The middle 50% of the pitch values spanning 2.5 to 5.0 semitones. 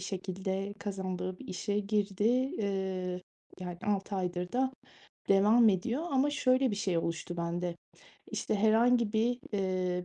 Yes: average, 3.2 semitones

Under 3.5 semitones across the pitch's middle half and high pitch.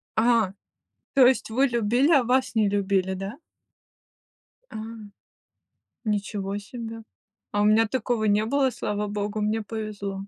Yes: average, 2.7 semitones; high, 215 Hz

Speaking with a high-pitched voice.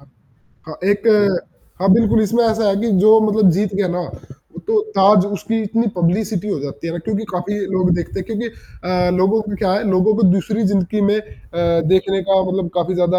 Yes: high, 195 Hz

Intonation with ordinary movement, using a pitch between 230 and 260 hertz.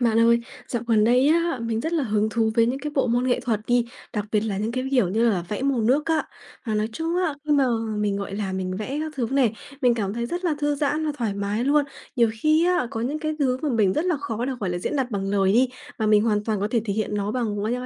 Yes: average, 4.8 semitones; high, 235 Hz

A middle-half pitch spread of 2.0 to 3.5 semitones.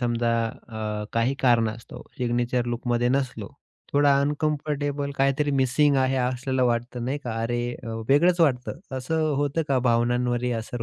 Yes: average, 2.8 semitones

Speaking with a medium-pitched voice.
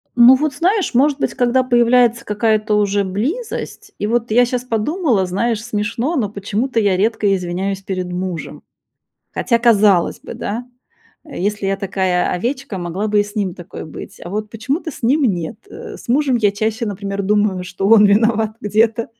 No: high, 215 Hz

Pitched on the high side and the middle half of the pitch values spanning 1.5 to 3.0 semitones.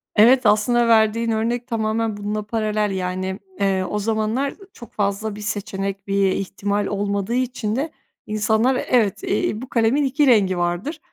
Yes: high, 215 Hz; narrow, 2.5 semitones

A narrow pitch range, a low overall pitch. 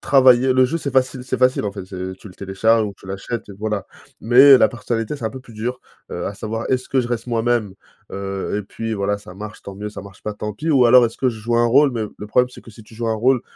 No: average, 3.5 semitones; low, 115 Hz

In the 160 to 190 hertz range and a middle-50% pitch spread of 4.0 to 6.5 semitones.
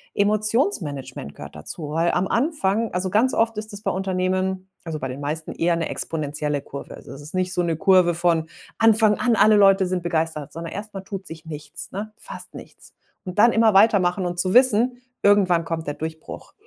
Yes: medium, 185 Hz; average, 4.3 semitones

